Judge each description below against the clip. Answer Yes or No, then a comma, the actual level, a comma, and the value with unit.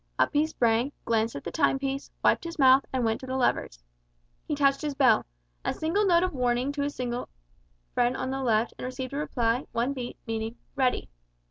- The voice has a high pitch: Yes, very high, 255 Hz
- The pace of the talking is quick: Yes, fast, 210 wpm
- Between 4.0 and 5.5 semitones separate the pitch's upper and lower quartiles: No, average, 2.8 semitones